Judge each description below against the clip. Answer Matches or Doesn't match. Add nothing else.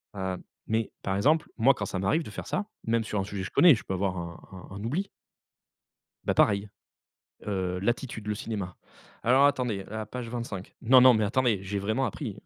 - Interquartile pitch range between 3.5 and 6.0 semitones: Matches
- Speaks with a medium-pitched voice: Doesn't match